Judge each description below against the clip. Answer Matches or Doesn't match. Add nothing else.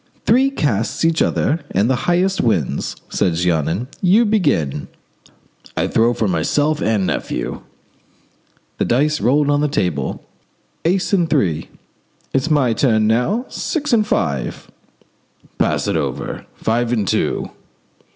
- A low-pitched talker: Matches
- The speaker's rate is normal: Doesn't match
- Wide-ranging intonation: Matches